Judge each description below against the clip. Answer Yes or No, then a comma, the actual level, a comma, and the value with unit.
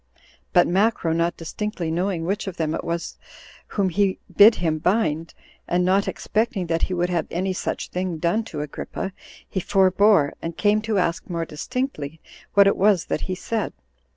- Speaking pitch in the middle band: Yes, medium, 180 Hz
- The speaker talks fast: No, average, 180 wpm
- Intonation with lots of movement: No, average, 3.3 semitones